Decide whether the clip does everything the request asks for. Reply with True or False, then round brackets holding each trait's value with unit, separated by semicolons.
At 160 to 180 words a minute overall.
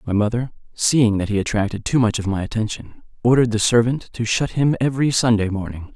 False (200 wpm)